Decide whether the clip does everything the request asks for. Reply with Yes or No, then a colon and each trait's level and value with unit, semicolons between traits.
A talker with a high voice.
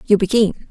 Yes: high, 205 Hz